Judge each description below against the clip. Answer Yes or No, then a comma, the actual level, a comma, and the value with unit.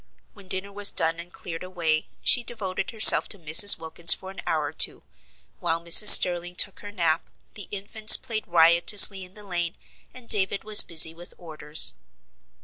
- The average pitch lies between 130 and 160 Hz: No, medium, 180 Hz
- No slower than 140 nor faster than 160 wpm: No, average, 175 wpm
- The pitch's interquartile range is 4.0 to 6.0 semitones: No, average, 3.6 semitones